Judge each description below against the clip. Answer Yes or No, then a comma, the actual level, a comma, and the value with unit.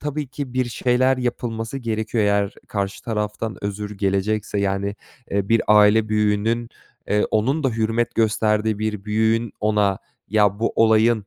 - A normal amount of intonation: No, narrow, 1.8 semitones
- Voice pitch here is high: No, low, 110 Hz